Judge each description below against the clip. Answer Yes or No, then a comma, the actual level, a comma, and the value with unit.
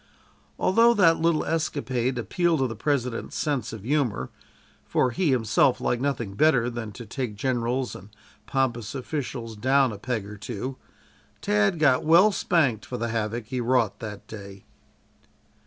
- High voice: No, low, 125 Hz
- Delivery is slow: No, average, 155 wpm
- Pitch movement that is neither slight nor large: Yes, average, 4.1 semitones